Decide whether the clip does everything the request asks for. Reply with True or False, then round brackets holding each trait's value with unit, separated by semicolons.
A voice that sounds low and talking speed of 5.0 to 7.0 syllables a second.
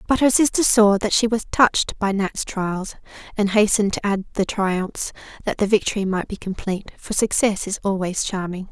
False (205 Hz; 5.2 syllables/s)